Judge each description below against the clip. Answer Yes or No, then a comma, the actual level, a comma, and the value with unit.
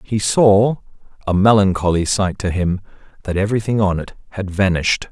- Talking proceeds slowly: Yes, slow, 130 wpm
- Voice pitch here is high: No, low, 100 Hz